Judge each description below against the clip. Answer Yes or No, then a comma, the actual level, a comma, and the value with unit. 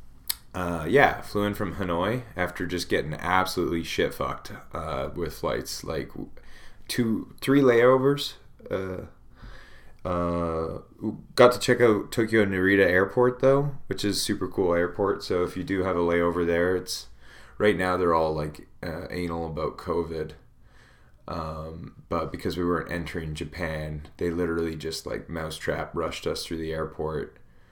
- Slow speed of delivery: No, average, 150 wpm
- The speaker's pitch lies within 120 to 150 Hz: No, very low, 90 Hz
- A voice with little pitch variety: No, average, 4.0 semitones